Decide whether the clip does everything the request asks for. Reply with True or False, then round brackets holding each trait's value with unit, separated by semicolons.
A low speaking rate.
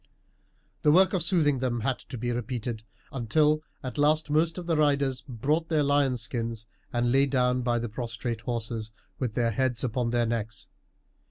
False (175 wpm)